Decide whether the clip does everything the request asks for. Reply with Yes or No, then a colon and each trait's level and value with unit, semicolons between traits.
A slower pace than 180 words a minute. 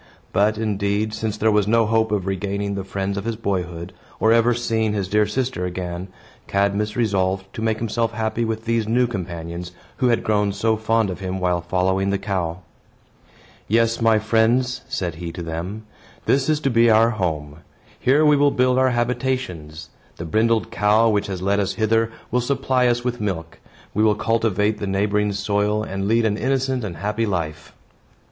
No: average, 185 wpm